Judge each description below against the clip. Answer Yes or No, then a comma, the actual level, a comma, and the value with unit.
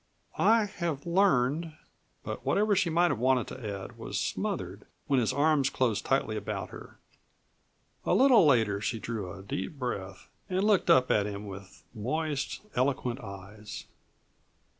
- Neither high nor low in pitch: No, low, 130 Hz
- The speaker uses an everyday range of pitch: No, wide, 7.6 semitones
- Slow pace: No, average, 155 wpm